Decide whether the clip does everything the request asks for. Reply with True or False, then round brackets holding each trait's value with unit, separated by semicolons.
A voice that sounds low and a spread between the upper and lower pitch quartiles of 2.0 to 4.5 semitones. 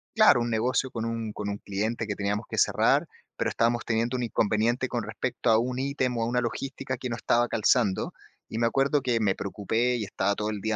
True (115 Hz; 2.5 semitones)